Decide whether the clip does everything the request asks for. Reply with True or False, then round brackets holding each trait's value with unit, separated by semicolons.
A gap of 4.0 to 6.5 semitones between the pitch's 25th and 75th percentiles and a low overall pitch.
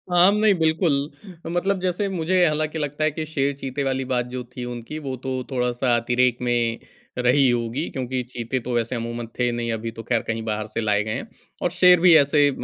True (4.6 semitones; 130 Hz)